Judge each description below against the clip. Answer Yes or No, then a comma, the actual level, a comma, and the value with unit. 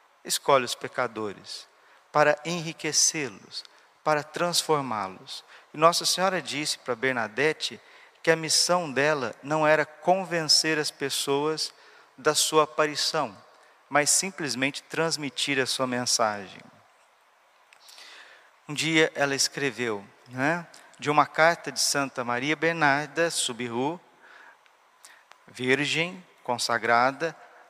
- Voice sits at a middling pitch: Yes, medium, 150 Hz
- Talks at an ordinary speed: No, slow, 100 wpm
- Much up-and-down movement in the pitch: No, average, 3.5 semitones